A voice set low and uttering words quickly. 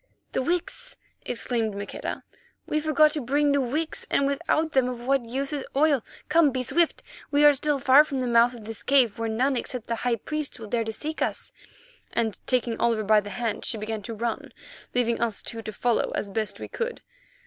No: very high, 250 Hz; fast, 210 wpm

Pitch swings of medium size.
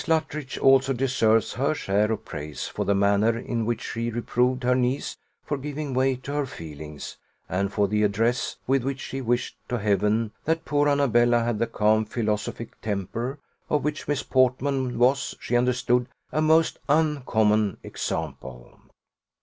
Yes: average, 4.1 semitones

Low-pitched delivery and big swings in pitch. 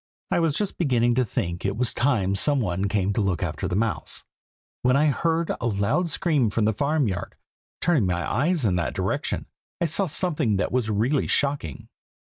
Yes: low, 120 Hz; wide, 6.9 semitones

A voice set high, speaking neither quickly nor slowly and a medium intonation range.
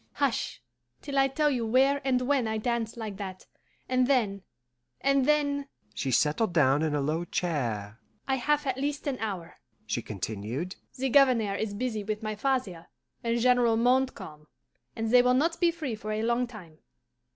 No: high, 230 Hz; average, 180 wpm; wide, 6.2 semitones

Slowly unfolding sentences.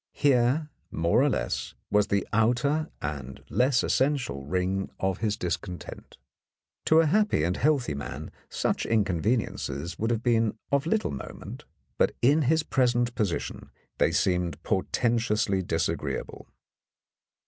Yes: slow, 125 wpm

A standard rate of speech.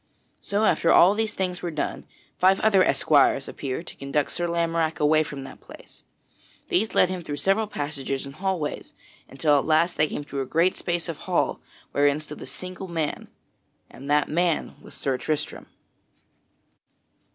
Yes: average, 170 wpm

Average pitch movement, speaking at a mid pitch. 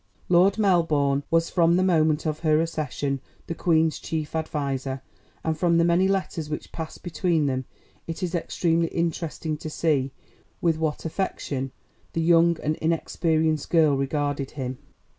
No: narrow, 2.2 semitones; medium, 160 Hz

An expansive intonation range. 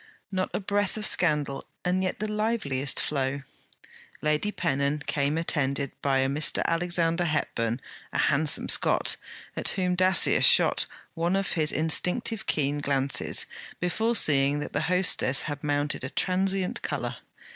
No: average, 4.8 semitones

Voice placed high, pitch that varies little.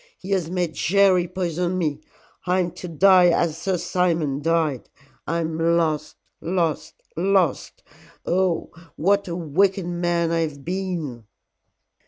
No: medium, 170 Hz; narrow, 2.3 semitones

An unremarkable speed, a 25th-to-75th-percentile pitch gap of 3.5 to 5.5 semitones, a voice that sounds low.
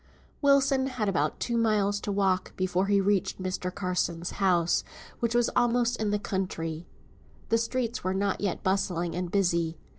No: average, 160 wpm; average, 4.1 semitones; high, 195 Hz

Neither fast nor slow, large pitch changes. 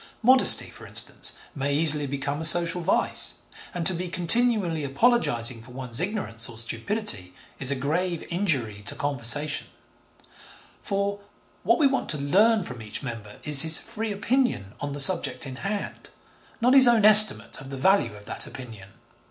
Yes: average, 165 wpm; wide, 7.9 semitones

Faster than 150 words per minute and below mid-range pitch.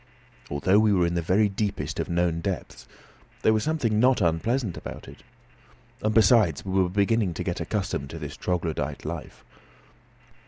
Yes: average, 165 wpm; very low, 95 Hz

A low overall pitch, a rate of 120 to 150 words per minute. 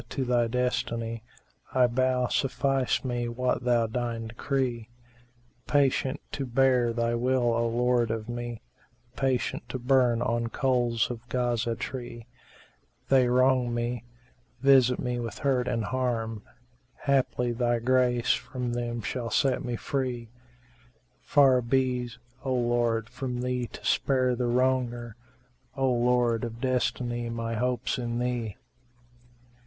Yes: low, 120 Hz; average, 140 wpm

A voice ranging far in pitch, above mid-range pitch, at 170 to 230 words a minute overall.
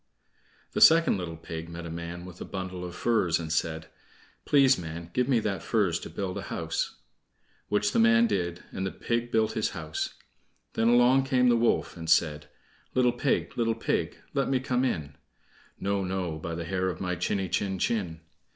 No: wide, 5.7 semitones; very low, 95 Hz; average, 190 wpm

